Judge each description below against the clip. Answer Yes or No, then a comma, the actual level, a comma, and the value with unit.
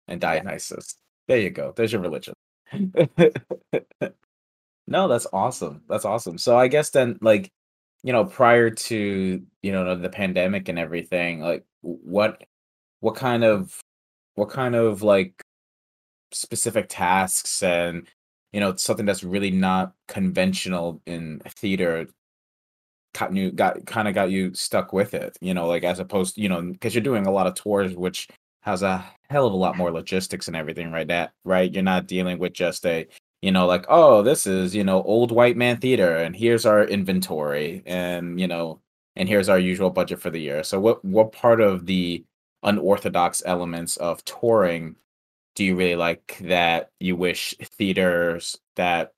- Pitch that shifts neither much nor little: Yes, average, 3.3 semitones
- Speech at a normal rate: Yes, average, 170 wpm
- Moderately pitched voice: No, very low, 95 Hz